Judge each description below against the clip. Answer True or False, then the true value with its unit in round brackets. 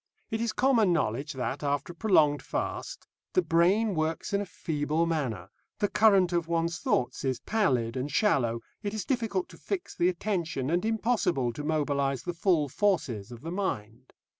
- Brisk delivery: False (175 wpm)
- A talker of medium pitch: True (165 Hz)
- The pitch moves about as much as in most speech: False (6.7 semitones)